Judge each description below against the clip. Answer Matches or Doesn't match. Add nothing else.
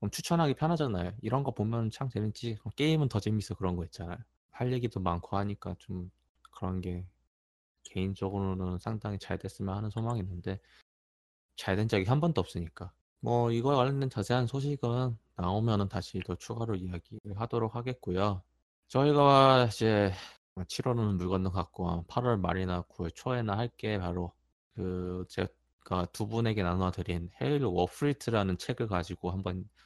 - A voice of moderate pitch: Doesn't match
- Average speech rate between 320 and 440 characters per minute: Matches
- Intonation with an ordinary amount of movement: Matches